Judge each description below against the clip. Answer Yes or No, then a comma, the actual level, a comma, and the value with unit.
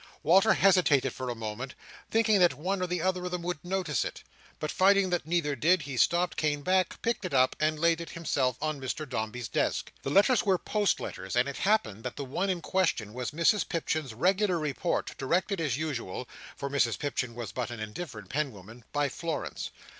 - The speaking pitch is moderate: Yes, medium, 155 Hz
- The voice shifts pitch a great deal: Yes, wide, 6.1 semitones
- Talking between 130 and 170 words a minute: No, average, 190 wpm